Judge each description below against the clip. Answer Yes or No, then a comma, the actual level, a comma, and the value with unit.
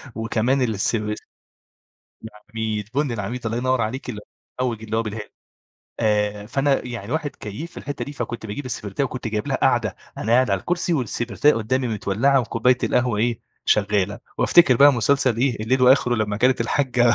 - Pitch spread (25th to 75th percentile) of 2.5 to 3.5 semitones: Yes, average, 3.2 semitones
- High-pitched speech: No, low, 120 Hz